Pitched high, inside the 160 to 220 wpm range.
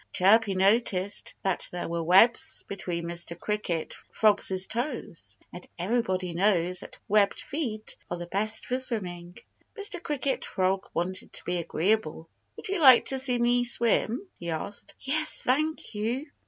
No: high, 205 Hz; average, 150 wpm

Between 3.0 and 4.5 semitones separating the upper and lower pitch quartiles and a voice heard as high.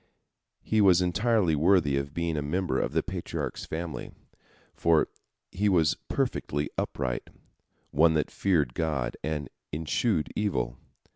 No: average, 4.0 semitones; very low, 80 Hz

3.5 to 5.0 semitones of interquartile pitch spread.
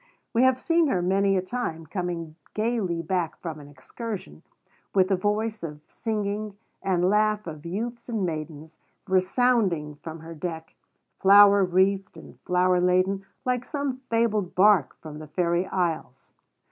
Yes: average, 4.2 semitones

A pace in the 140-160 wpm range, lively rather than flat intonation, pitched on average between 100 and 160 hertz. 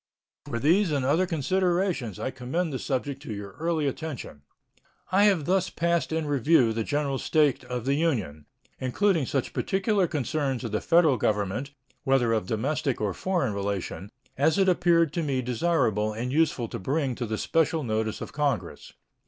No: average, 170 wpm; wide, 6.0 semitones; medium, 140 Hz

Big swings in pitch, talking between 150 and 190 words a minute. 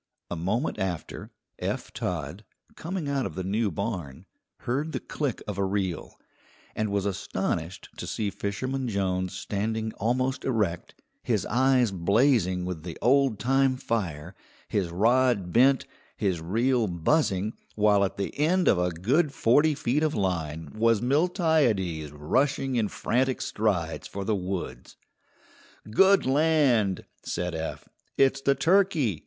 No: wide, 6.4 semitones; average, 140 wpm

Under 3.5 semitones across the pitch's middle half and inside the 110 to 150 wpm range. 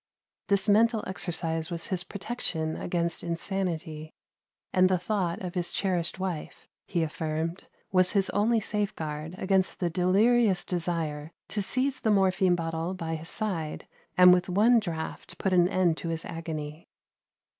Yes: average, 2.9 semitones; average, 145 wpm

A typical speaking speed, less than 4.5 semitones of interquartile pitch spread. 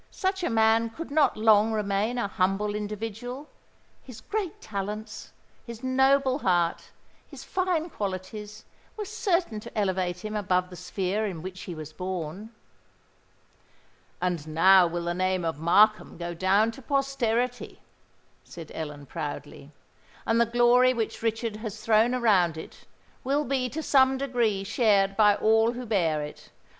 No: average, 145 wpm; average, 4.9 semitones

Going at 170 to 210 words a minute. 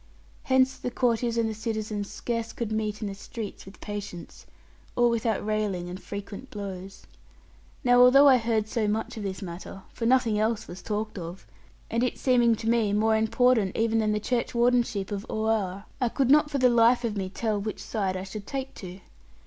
Yes: average, 195 wpm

